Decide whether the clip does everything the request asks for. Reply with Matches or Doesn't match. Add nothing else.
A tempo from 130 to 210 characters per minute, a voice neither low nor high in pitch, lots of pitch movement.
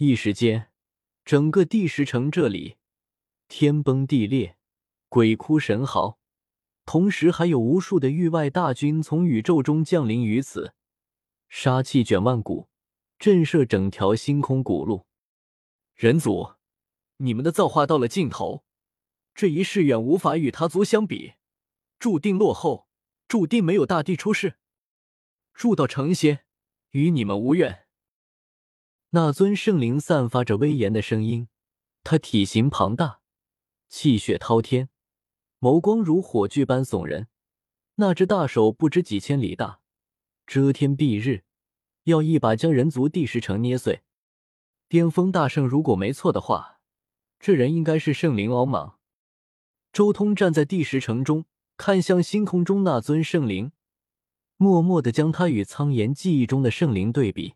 Matches